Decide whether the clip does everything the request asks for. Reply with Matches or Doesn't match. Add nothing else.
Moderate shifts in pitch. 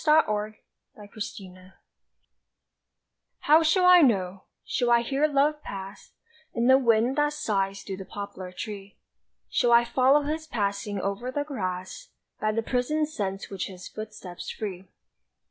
Doesn't match